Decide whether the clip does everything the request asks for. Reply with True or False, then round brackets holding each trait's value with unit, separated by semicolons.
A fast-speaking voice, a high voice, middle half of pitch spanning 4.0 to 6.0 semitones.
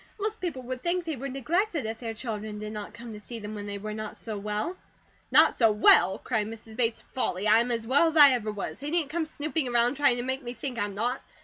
True (255 wpm; 240 Hz; 4.8 semitones)